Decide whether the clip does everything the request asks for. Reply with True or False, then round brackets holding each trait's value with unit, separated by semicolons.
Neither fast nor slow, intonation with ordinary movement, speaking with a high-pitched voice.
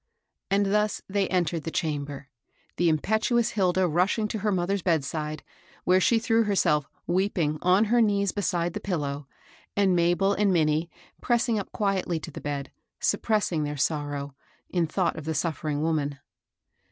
False (160 wpm; 4.7 semitones; 175 Hz)